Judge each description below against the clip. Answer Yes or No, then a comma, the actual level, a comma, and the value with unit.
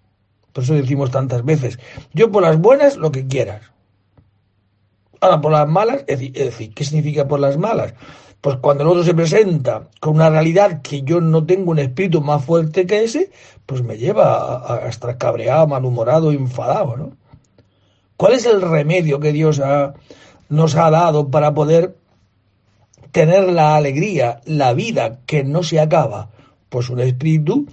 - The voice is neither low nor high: Yes, medium, 150 Hz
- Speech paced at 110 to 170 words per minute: Yes, average, 165 wpm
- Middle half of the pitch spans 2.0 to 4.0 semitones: No, average, 4.5 semitones